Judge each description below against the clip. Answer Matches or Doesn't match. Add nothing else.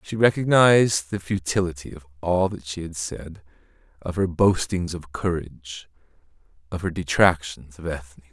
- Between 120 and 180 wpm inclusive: Matches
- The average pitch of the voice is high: Doesn't match